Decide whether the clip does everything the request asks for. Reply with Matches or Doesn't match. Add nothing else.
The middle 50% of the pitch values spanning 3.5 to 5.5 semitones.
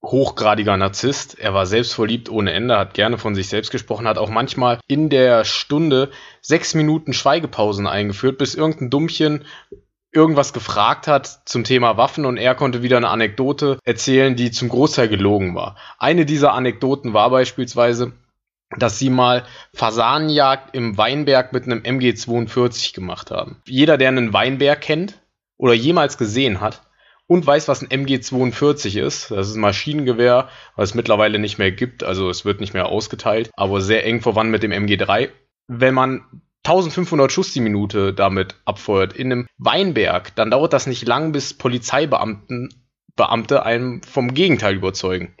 Matches